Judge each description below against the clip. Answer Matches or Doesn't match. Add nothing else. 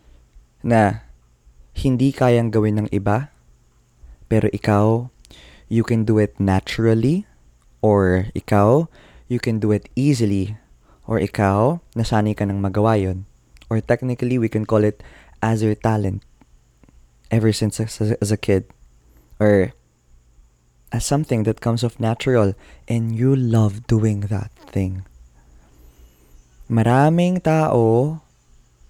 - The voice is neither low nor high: Doesn't match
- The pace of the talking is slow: Doesn't match